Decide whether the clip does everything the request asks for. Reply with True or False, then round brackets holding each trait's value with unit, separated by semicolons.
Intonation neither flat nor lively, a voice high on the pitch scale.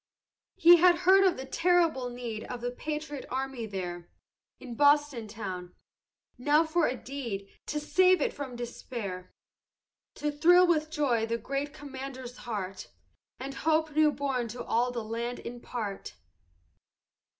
True (4.4 semitones; 260 Hz)